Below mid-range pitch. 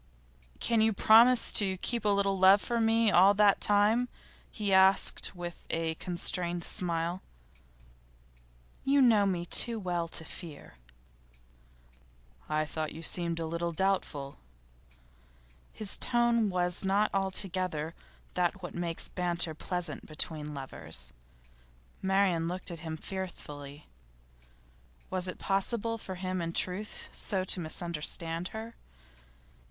No: medium, 185 Hz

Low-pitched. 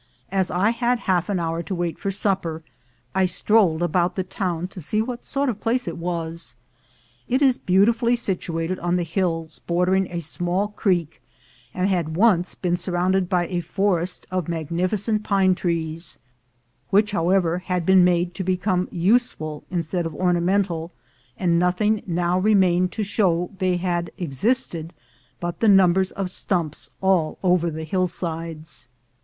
No: medium, 180 Hz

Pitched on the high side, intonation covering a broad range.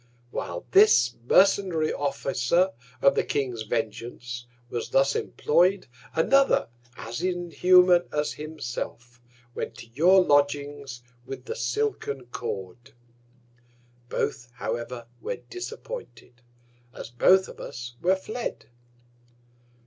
No: medium, 145 Hz; wide, 7.3 semitones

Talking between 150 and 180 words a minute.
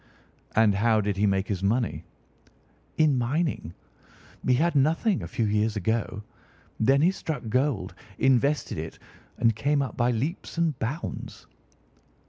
No: average, 140 wpm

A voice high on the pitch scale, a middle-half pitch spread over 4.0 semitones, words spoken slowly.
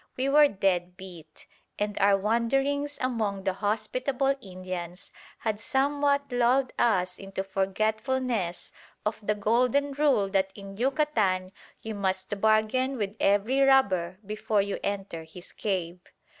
Yes: high, 210 Hz; average, 5.1 semitones; slow, 130 wpm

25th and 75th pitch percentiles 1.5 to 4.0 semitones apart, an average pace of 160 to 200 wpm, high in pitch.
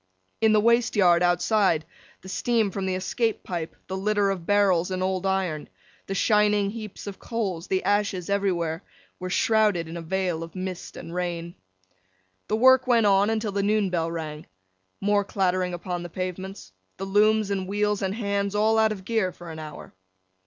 Yes: average, 2.8 semitones; average, 180 wpm; high, 195 Hz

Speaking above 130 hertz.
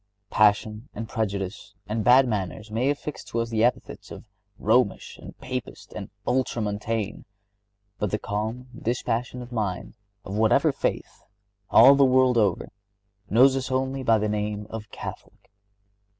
No: low, 115 Hz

